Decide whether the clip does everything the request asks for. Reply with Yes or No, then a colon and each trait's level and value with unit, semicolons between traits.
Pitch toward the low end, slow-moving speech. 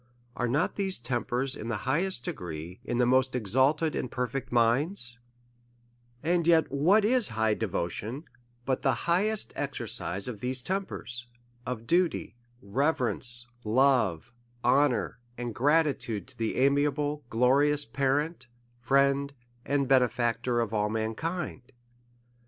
Yes: low, 130 Hz; slow, 130 wpm